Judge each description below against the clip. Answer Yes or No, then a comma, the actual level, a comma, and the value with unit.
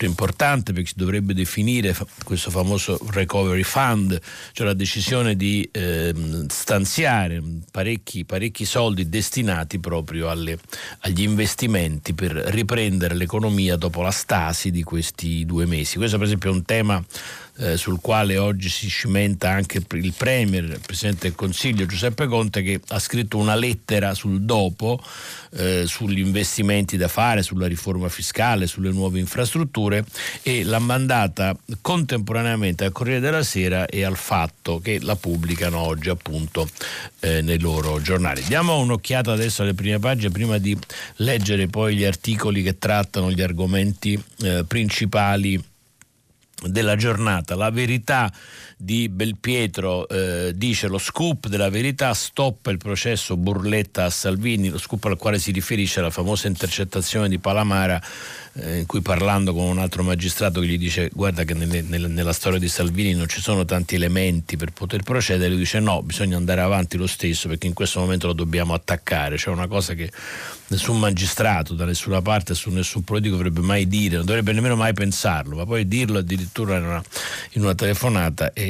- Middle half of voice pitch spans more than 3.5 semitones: No, average, 3.1 semitones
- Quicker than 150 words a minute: Yes, average, 160 wpm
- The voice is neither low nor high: No, very low, 95 Hz